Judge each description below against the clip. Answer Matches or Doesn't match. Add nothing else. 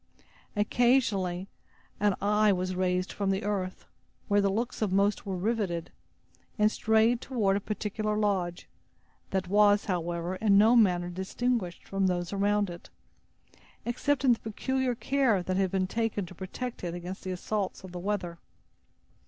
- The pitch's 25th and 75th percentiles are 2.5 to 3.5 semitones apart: Matches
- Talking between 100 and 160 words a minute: Matches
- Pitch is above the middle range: Matches